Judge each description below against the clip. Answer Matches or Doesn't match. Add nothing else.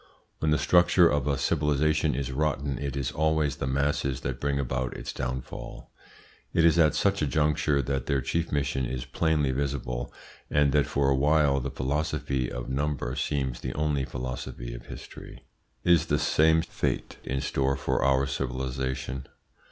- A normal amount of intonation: Doesn't match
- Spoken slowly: Doesn't match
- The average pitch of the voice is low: Matches